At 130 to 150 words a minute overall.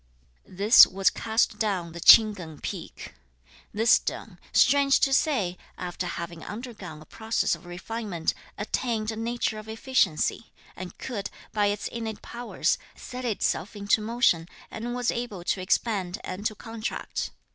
Yes: average, 145 wpm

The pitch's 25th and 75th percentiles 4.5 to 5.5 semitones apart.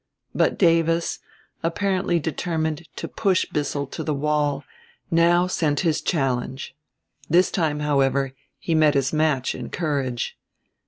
No: average, 3.0 semitones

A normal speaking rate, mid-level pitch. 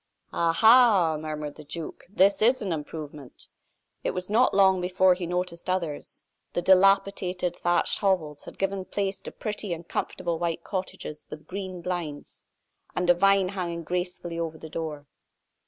Yes: average, 155 wpm; medium, 180 Hz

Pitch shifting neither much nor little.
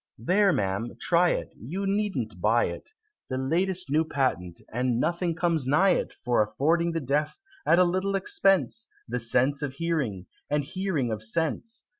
No: wide, 6.2 semitones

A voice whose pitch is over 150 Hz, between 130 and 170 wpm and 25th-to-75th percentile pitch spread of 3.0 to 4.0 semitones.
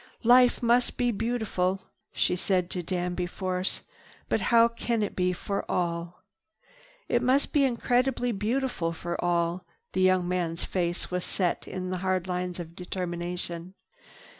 No: medium, 185 Hz; average, 140 wpm; average, 4.8 semitones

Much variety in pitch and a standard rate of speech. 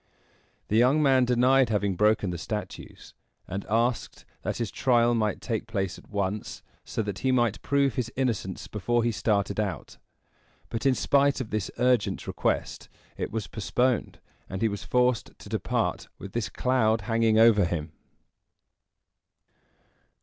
No: average, 3.4 semitones; average, 150 wpm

